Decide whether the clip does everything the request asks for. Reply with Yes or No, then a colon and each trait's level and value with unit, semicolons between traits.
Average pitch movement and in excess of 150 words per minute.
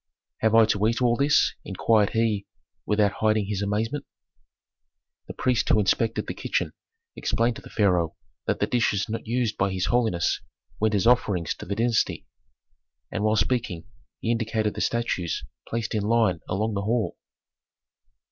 No: narrow, 2.3 semitones; average, 160 wpm